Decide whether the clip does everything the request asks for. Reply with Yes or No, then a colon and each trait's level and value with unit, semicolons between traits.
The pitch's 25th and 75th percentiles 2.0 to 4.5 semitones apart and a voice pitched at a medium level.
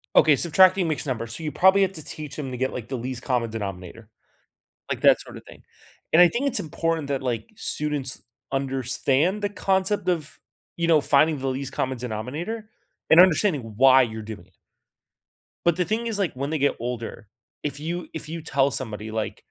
No: average, 5.3 semitones; medium, 145 Hz